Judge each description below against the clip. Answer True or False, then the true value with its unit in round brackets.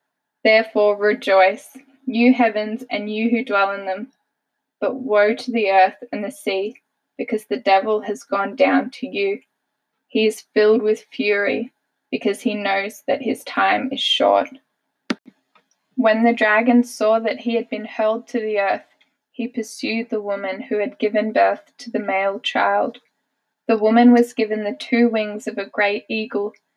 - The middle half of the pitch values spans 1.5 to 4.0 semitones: True (2.5 semitones)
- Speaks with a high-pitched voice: True (220 Hz)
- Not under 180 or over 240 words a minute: False (165 wpm)